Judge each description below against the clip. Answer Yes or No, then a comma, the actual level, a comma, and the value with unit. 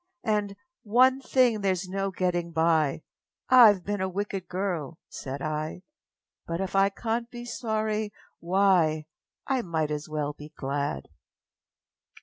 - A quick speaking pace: No, slow, 135 wpm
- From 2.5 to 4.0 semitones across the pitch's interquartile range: No, average, 5.2 semitones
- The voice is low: No, high, 190 Hz